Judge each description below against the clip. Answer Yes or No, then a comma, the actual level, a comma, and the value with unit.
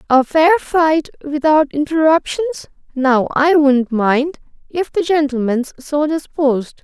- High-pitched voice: Yes, very high, 295 Hz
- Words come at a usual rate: No, slow, 125 wpm